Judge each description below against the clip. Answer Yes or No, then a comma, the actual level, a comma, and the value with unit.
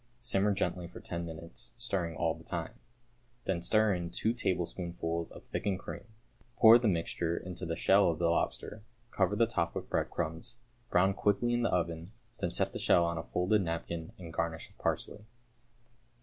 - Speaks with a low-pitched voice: Yes, very low, 90 Hz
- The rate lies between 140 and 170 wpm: No, average, 180 wpm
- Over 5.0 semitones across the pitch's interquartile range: No, average, 3.5 semitones